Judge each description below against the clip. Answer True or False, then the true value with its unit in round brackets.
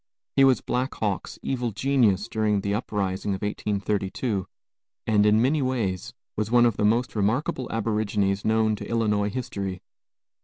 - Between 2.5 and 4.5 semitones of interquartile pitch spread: True (3.0 semitones)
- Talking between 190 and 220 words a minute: False (150 wpm)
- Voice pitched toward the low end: True (105 Hz)